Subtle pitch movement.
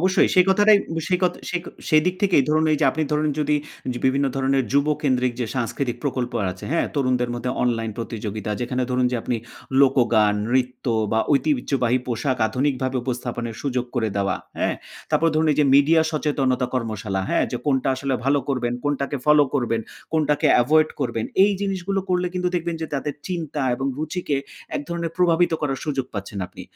No: average, 4.1 semitones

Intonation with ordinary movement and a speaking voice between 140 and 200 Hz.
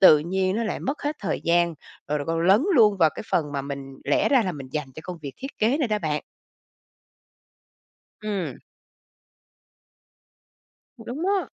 No: wide, 6.9 semitones; medium, 185 Hz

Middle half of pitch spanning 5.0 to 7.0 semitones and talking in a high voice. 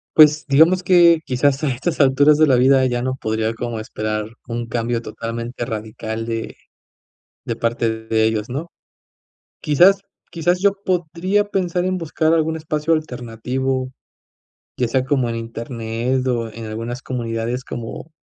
No: average, 5.3 semitones; low, 125 Hz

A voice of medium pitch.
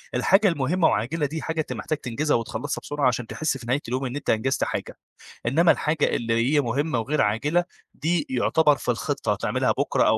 Yes: medium, 145 Hz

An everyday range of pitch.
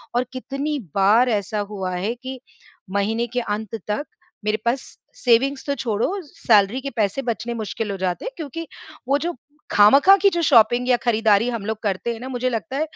Yes: average, 3.8 semitones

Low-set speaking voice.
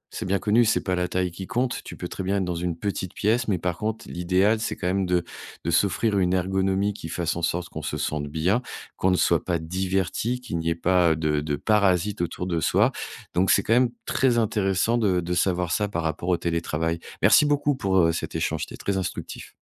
Yes: very low, 90 Hz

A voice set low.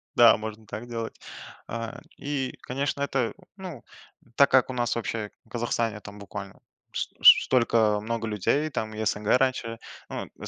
Yes: low, 115 Hz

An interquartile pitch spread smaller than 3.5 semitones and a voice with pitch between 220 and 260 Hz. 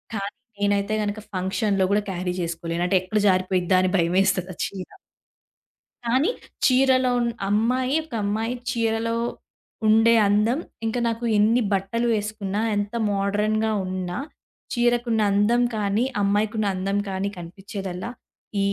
No: average, 3.1 semitones; high, 205 Hz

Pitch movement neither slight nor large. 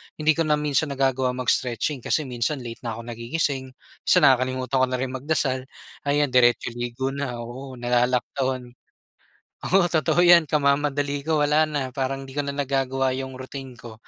No: narrow, 2.3 semitones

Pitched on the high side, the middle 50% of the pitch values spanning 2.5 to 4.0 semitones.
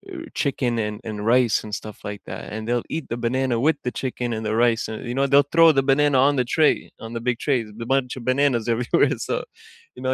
No: low, 125 Hz; average, 3.1 semitones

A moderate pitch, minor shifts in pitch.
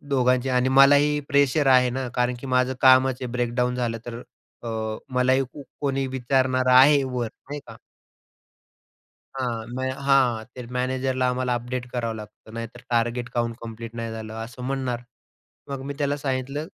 No: low, 125 Hz; narrow, 1.9 semitones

